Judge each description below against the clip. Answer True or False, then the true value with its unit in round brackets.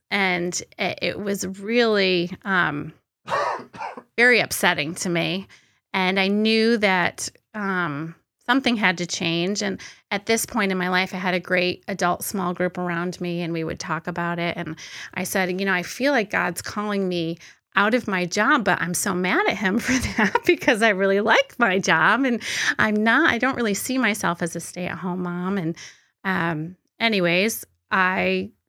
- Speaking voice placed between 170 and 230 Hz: True (185 Hz)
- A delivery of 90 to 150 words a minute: False (180 wpm)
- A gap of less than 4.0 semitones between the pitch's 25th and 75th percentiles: True (3.3 semitones)